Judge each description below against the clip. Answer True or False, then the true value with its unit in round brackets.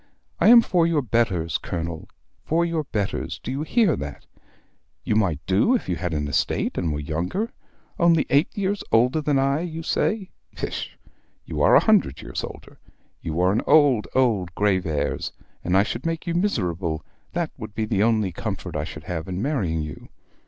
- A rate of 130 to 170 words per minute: False (185 wpm)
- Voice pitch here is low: True (110 Hz)